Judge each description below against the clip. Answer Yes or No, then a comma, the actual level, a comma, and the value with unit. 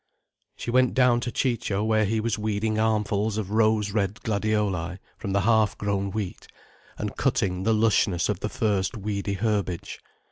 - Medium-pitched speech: No, low, 105 Hz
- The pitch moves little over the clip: Yes, narrow, 1.9 semitones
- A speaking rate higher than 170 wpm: No, average, 165 wpm